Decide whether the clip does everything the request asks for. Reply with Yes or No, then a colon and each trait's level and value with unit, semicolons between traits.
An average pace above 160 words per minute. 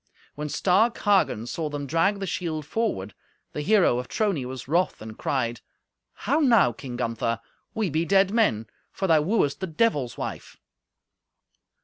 No: average, 155 wpm